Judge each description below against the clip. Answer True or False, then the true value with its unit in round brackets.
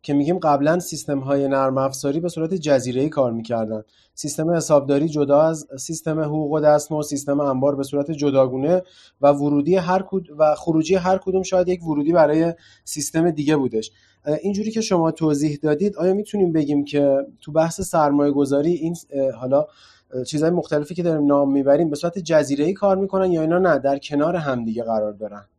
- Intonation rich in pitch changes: False (3.3 semitones)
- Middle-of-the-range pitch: True (150 Hz)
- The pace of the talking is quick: True (180 wpm)